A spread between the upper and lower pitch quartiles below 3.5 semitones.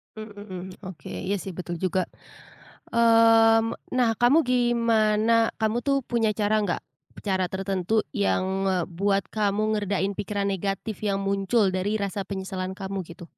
Yes: average, 2.8 semitones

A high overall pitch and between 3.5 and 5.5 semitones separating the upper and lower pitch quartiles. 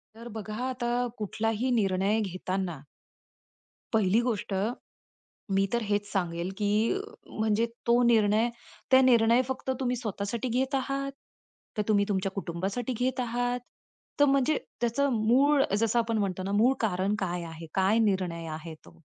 Yes: high, 220 Hz; average, 4.1 semitones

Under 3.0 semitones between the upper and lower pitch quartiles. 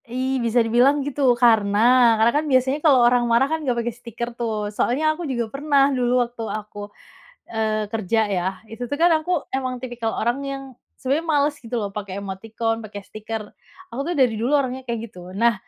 No: average, 3.3 semitones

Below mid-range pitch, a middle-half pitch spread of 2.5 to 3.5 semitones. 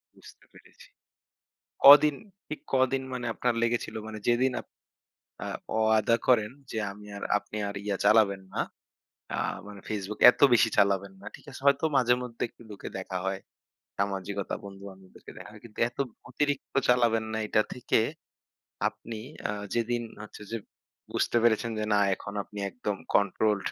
Yes: low, 110 Hz; average, 3.2 semitones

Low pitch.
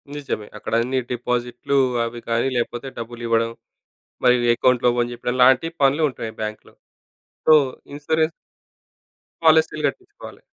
Yes: low, 125 Hz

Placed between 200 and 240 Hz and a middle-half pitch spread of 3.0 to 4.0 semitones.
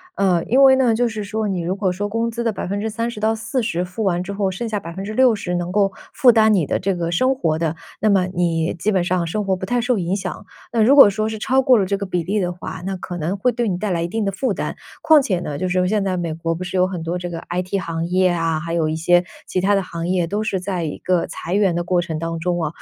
No: medium, 185 Hz; average, 3.7 semitones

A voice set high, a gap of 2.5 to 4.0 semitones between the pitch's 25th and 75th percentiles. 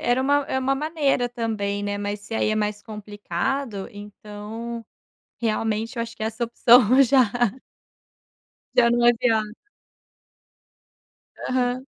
Yes: high, 230 Hz; average, 3.2 semitones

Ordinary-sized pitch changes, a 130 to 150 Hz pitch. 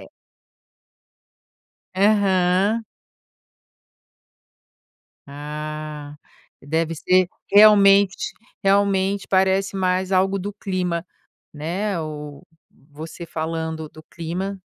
No: average, 3.7 semitones; medium, 185 Hz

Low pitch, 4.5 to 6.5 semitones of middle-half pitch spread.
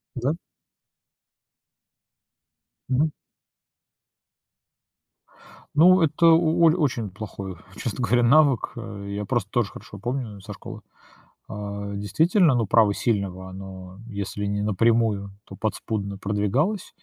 Yes: low, 110 Hz; average, 5.1 semitones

